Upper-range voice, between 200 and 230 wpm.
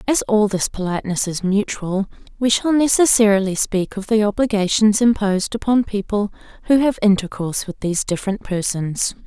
No: high, 205 Hz; average, 150 wpm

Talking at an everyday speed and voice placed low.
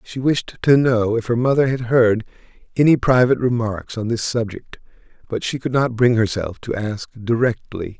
Yes: average, 180 wpm; low, 120 Hz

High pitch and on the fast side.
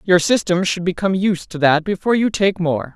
No: medium, 180 Hz; fast, 225 wpm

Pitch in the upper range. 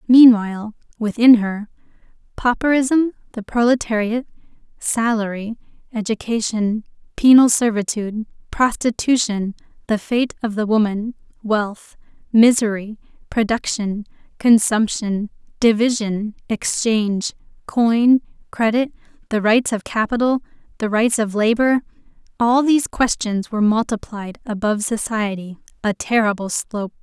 Yes: high, 225 Hz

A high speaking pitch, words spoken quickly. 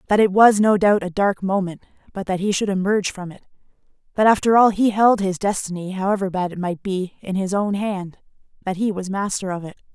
Yes: high, 195 Hz; fast, 225 wpm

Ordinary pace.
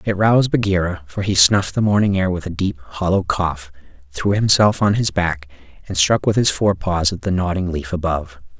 No: fast, 210 wpm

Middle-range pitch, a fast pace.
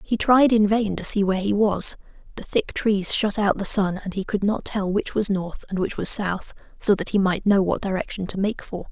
No: high, 200 Hz; fast, 255 wpm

